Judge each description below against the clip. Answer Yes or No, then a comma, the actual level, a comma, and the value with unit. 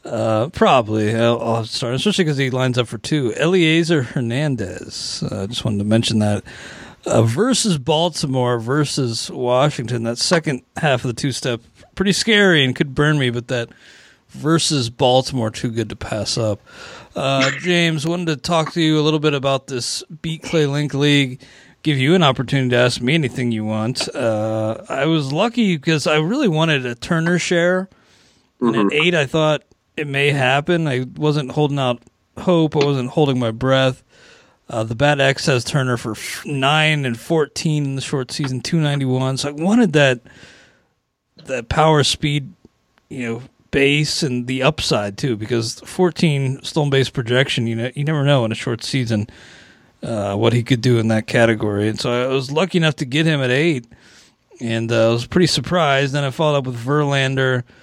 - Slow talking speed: No, average, 185 wpm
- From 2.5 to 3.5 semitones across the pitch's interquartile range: No, average, 4.4 semitones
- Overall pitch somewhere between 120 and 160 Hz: Yes, low, 135 Hz